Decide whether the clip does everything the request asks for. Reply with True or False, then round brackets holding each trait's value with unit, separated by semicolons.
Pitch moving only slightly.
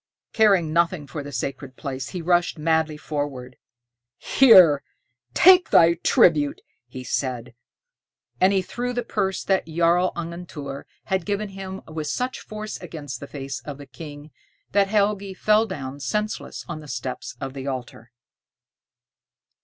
False (5.5 semitones)